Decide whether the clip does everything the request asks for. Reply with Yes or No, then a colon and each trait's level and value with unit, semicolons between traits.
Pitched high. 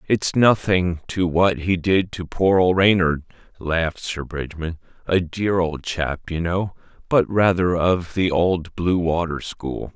No: very low, 90 Hz